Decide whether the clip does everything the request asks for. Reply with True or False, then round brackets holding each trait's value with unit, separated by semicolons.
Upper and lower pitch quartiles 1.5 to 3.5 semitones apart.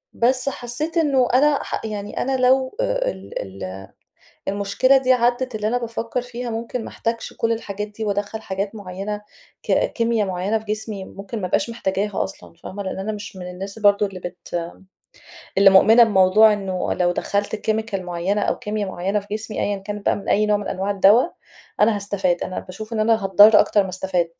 True (3.0 semitones)